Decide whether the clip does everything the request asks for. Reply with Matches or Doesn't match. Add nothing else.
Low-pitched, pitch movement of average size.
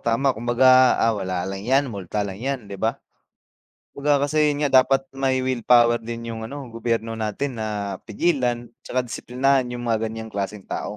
Matches